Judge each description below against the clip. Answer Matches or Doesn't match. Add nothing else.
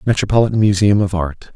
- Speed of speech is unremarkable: Matches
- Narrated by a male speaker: Matches